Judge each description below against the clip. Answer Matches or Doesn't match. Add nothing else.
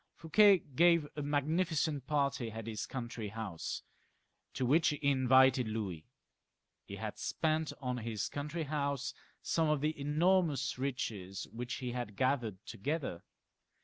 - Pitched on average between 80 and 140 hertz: Matches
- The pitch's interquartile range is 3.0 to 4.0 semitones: Doesn't match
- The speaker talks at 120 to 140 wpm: Matches